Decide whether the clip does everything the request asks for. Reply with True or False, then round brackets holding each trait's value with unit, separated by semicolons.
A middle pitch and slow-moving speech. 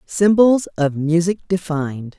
True (170 Hz; 110 wpm)